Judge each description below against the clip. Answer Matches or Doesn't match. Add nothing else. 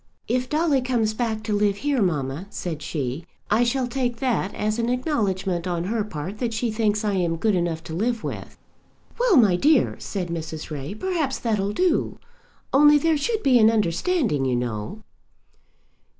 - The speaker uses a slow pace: Doesn't match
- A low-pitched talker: Doesn't match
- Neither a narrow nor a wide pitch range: Doesn't match